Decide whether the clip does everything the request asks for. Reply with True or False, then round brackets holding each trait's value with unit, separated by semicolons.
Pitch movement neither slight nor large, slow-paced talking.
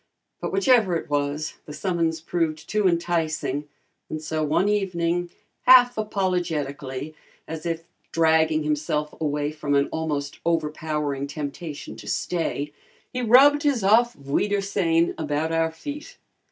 True (3.9 semitones; 125 wpm)